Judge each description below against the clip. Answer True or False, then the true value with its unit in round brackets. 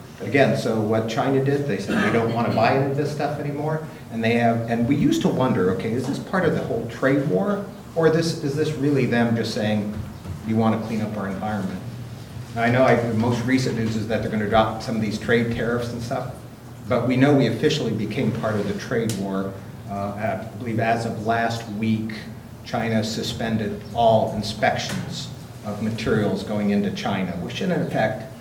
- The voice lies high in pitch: False (115 Hz)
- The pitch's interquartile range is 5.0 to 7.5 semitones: False (2.8 semitones)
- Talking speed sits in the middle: False (210 wpm)